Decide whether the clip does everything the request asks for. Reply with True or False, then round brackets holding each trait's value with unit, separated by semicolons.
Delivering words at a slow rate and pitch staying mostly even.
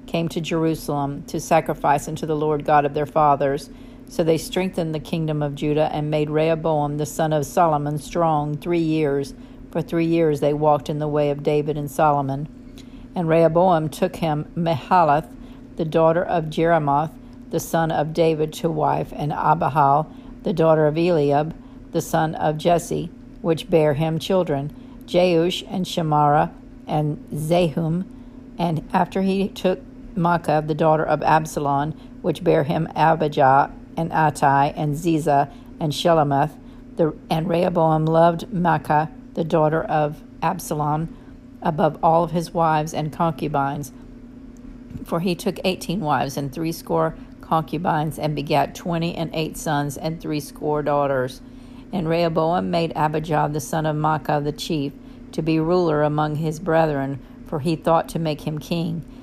False (150 wpm; 2.2 semitones)